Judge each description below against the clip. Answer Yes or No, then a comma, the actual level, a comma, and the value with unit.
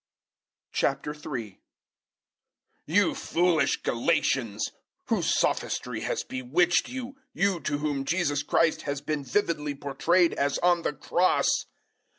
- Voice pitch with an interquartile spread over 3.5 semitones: Yes, average, 4.0 semitones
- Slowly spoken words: Yes, slow, 110 wpm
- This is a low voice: No, medium, 150 Hz